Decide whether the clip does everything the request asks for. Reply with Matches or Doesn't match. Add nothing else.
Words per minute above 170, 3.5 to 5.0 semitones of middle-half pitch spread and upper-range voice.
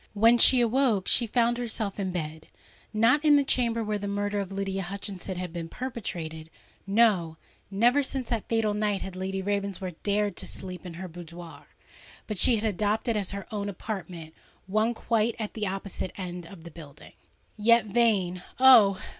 Doesn't match